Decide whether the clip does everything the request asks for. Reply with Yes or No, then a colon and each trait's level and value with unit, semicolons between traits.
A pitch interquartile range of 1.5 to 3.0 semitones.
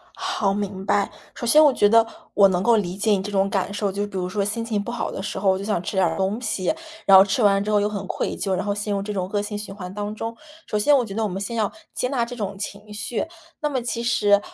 Yes: narrow, 2.4 semitones